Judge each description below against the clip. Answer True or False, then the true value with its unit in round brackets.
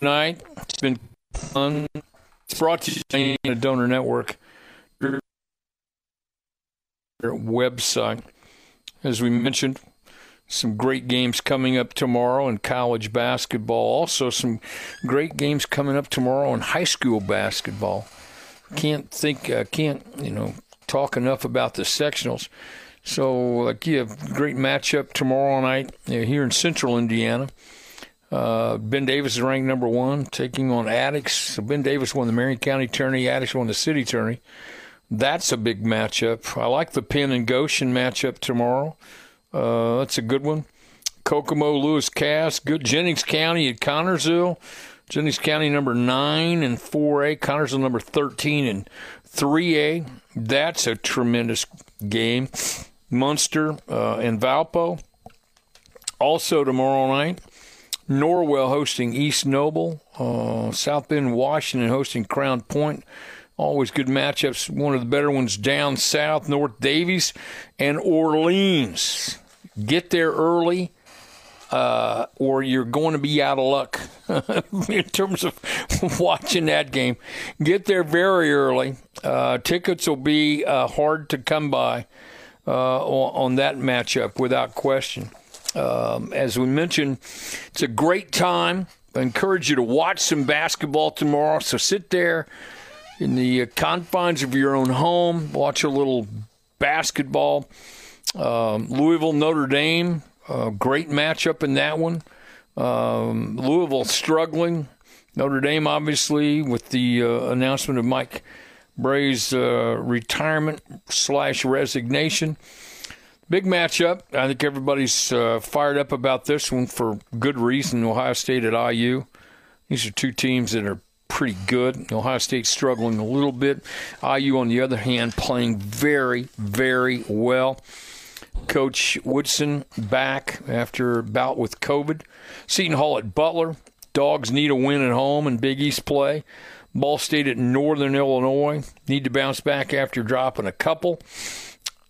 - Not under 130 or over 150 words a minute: True (140 wpm)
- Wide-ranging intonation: False (3.1 semitones)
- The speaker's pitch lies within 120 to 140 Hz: True (135 Hz)